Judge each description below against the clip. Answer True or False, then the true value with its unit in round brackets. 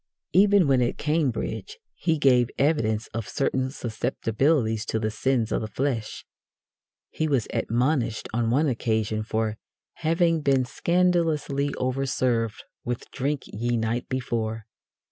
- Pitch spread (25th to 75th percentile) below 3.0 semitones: False (4.6 semitones)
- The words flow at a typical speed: False (125 wpm)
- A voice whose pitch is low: True (125 Hz)